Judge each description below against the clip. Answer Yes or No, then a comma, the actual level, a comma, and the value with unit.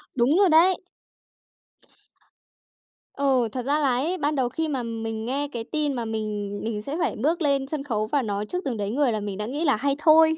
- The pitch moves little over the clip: No, average, 5.1 semitones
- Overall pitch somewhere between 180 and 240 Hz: No, very high, 265 Hz